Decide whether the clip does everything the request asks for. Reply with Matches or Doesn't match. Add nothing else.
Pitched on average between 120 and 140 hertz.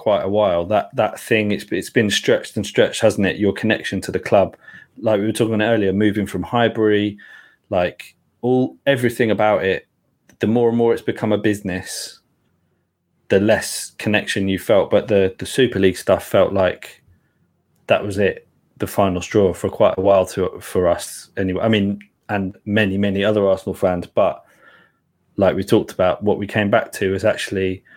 Doesn't match